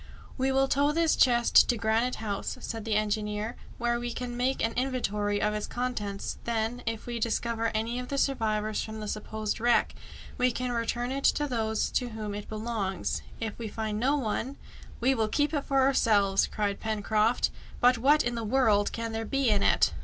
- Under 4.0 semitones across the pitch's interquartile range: Yes, average, 2.8 semitones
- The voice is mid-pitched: No, high, 230 Hz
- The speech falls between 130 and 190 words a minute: No, average, 200 wpm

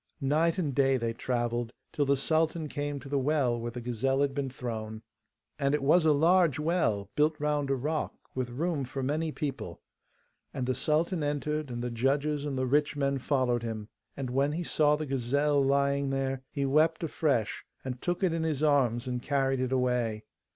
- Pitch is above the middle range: No, medium, 140 Hz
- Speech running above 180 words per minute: Yes, average, 195 wpm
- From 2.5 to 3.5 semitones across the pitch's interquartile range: Yes, average, 3.1 semitones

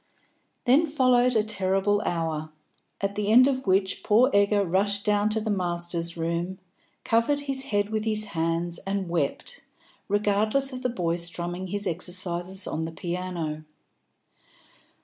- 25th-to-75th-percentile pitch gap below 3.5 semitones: No, average, 3.9 semitones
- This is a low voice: No, high, 195 Hz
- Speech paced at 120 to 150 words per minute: Yes, average, 145 wpm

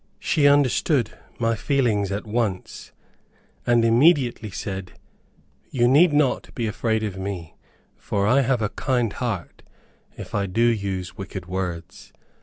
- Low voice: Yes, low, 110 Hz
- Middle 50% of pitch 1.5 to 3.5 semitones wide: No, average, 4.1 semitones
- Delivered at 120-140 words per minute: Yes, slow, 135 wpm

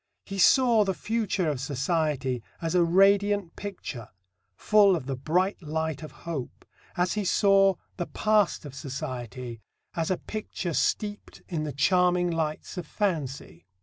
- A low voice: No, medium, 170 Hz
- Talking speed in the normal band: Yes, average, 150 wpm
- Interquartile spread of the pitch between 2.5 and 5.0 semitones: No, wide, 5.4 semitones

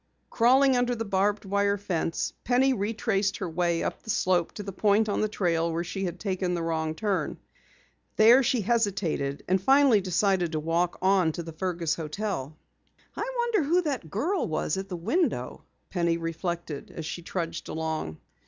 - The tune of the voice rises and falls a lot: No, average, 4.6 semitones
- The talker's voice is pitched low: No, high, 190 Hz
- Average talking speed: Yes, average, 175 wpm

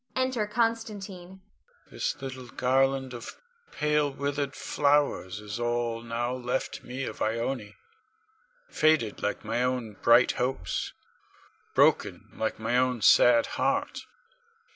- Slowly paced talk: Yes, slow, 120 wpm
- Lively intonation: No, average, 4.2 semitones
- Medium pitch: No, low, 130 Hz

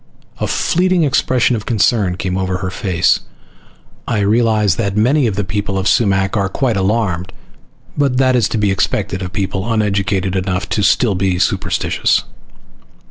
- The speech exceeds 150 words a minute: Yes, average, 160 wpm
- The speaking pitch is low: Yes, low, 100 Hz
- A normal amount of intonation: Yes, average, 3.4 semitones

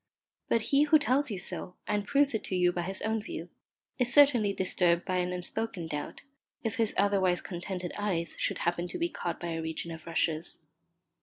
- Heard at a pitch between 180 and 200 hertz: Yes, high, 190 Hz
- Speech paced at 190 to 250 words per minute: Yes, average, 200 wpm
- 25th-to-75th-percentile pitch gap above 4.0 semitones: Yes, average, 4.5 semitones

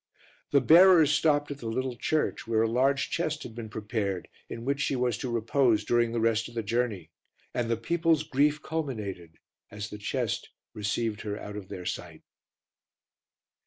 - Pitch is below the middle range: Yes, low, 120 Hz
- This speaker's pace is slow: No, average, 175 wpm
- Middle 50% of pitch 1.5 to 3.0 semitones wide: No, average, 4.7 semitones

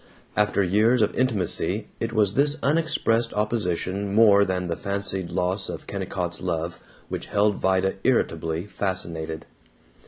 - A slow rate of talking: Yes, slow, 130 wpm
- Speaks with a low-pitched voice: Yes, low, 100 Hz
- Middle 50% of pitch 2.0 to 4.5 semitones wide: Yes, average, 3.3 semitones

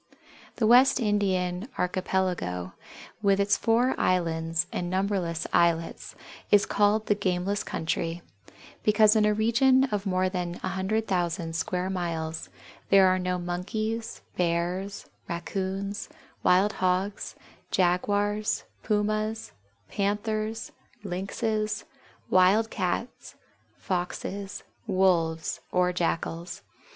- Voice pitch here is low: No, high, 190 Hz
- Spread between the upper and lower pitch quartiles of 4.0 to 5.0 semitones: No, average, 2.9 semitones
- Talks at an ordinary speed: No, slow, 100 wpm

